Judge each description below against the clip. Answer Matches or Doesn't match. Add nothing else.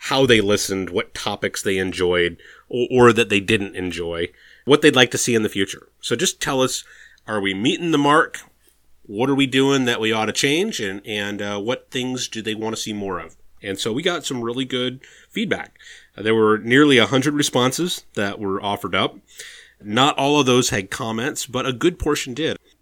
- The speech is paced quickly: Matches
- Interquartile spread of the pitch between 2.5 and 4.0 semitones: Doesn't match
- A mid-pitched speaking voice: Doesn't match